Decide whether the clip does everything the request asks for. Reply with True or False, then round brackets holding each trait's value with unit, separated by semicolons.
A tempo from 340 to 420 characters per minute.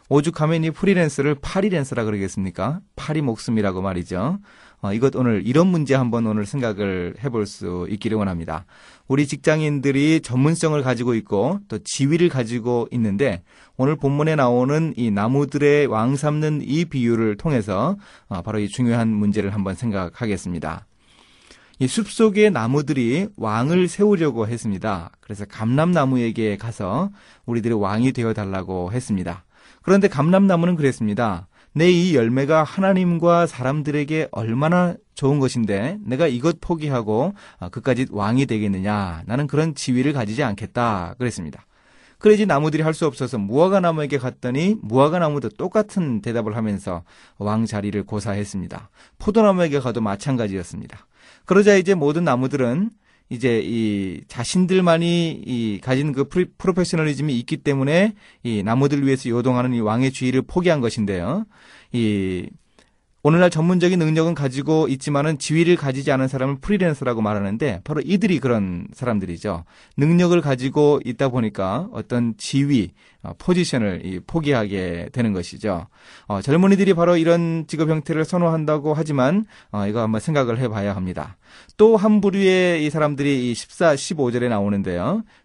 True (345 characters per minute)